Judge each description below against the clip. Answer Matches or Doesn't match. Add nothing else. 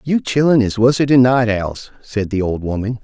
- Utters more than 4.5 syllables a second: Matches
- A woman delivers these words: Doesn't match